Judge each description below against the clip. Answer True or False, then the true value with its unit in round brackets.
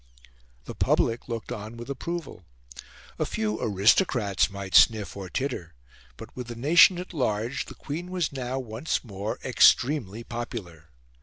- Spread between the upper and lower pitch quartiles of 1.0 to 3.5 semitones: False (5.1 semitones)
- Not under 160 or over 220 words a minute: False (145 wpm)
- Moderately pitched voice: False (115 Hz)